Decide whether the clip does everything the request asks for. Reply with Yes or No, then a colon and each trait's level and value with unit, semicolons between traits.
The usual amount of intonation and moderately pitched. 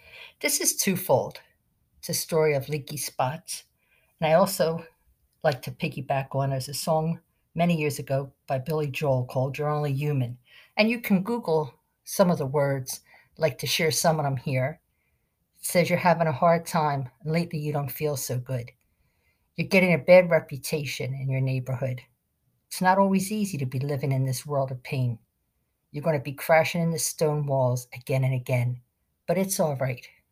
Yes: average, 3.9 semitones; medium, 145 Hz